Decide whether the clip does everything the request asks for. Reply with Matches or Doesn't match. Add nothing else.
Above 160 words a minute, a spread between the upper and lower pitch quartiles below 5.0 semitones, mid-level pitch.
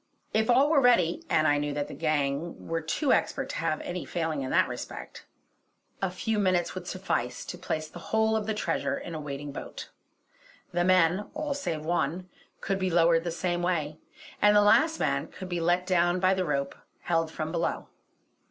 Matches